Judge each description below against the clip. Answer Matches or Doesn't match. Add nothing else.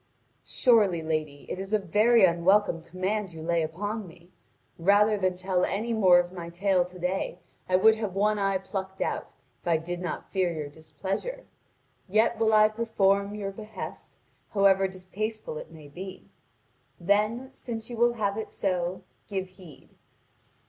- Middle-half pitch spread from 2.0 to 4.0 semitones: Matches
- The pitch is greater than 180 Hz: Matches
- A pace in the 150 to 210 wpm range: Matches